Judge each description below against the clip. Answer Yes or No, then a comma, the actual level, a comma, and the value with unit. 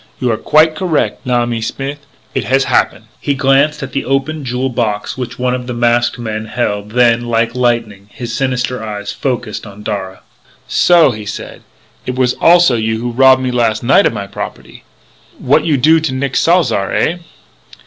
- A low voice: Yes, low, 125 Hz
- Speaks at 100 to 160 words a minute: No, average, 180 wpm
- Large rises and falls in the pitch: No, average, 3.3 semitones